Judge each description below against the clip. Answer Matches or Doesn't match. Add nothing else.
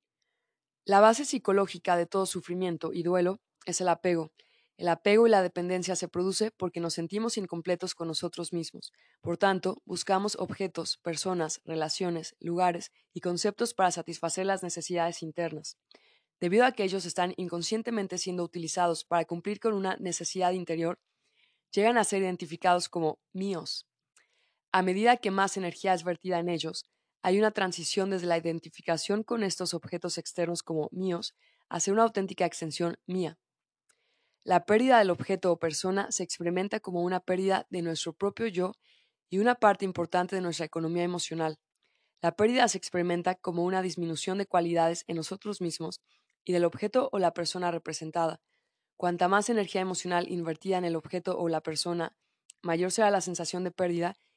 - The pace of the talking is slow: Doesn't match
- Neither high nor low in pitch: Matches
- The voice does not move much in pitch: Matches